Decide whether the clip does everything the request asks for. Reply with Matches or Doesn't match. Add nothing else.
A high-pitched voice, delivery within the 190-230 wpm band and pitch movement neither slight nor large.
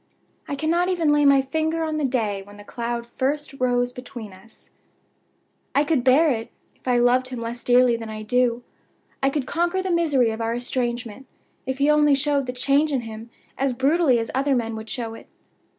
Matches